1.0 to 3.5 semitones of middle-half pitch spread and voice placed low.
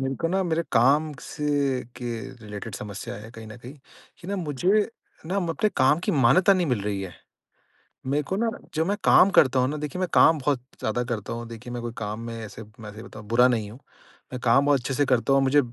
No: average, 4.8 semitones; low, 130 Hz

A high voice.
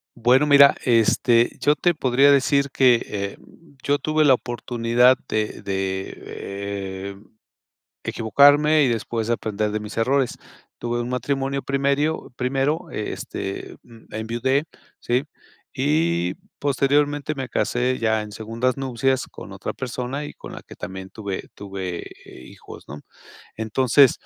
No: low, 120 Hz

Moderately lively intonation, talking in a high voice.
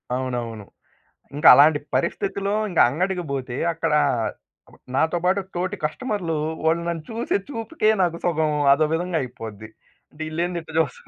No: average, 4.3 semitones; medium, 160 Hz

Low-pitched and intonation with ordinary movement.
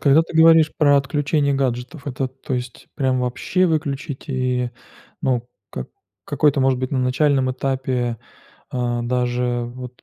No: low, 130 Hz; narrow, 2.3 semitones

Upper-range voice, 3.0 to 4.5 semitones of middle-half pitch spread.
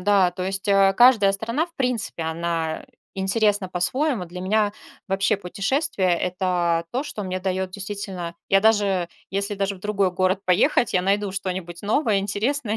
No: high, 195 Hz; narrow, 2.4 semitones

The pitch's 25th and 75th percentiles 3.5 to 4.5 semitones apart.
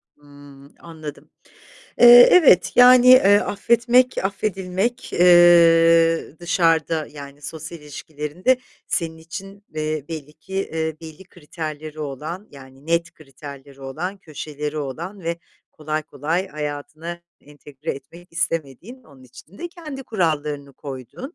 Yes: average, 4.2 semitones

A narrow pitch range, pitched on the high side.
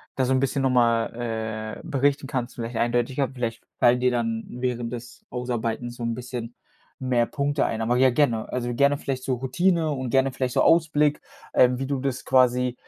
No: narrow, 2.1 semitones; low, 125 Hz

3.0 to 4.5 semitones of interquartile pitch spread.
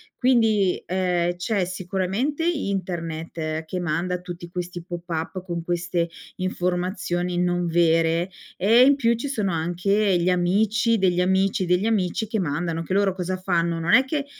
No: narrow, 2.5 semitones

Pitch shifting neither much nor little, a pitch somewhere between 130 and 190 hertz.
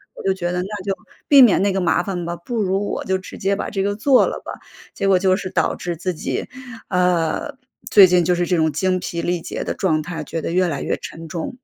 No: narrow, 2.2 semitones; medium, 185 Hz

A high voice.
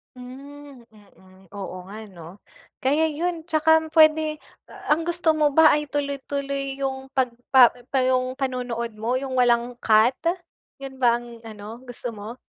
Yes: very high, 260 Hz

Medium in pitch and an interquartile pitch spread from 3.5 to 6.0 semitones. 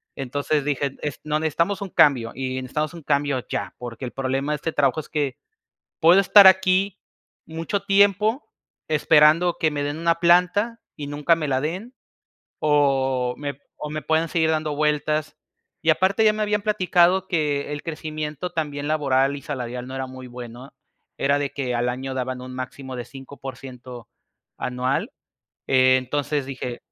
Yes: medium, 145 Hz; average, 4.0 semitones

